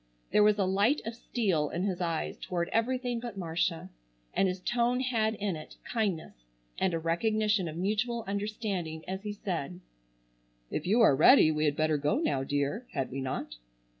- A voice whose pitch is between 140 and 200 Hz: Yes, high, 190 Hz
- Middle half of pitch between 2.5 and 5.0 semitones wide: No, wide, 5.4 semitones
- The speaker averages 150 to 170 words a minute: No, average, 180 wpm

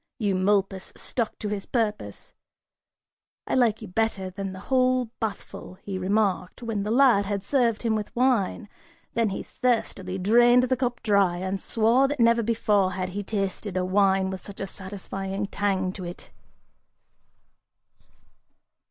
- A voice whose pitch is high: Yes, high, 205 Hz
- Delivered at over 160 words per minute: No, average, 150 wpm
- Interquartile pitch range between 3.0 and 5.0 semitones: Yes, average, 3.4 semitones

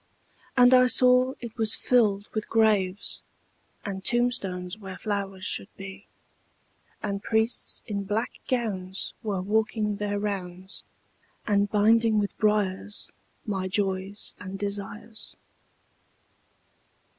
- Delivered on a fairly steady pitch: Yes, narrow, 2.3 semitones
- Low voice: No, high, 205 Hz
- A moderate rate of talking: No, slow, 110 wpm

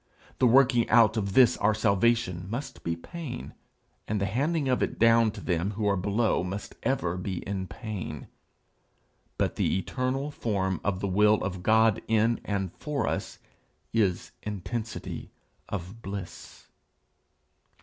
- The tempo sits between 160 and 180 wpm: No, average, 145 wpm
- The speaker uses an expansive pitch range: No, average, 3.6 semitones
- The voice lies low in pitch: Yes, low, 105 Hz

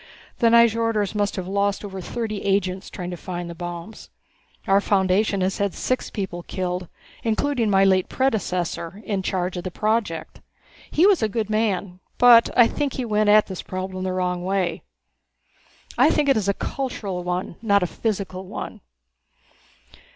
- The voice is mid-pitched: No, high, 195 Hz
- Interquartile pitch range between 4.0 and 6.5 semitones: No, average, 3.2 semitones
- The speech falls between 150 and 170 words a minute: Yes, average, 165 wpm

